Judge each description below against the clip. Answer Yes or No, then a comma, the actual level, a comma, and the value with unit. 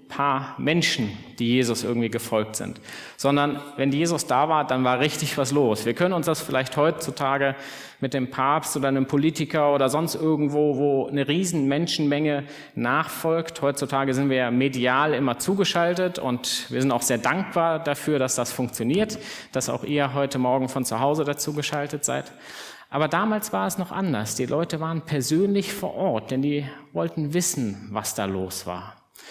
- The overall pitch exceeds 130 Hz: Yes, medium, 140 Hz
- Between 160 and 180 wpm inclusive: Yes, average, 170 wpm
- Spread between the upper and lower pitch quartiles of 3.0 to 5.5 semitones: Yes, average, 3.4 semitones